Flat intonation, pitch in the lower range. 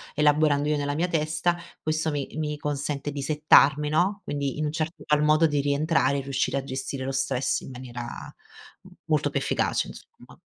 No: narrow, 1.9 semitones; medium, 150 Hz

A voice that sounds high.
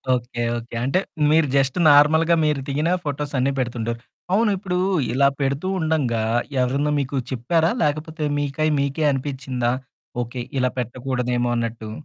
No: medium, 140 Hz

